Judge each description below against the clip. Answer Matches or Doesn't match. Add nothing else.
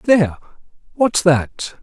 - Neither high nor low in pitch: Matches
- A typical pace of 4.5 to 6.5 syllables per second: Doesn't match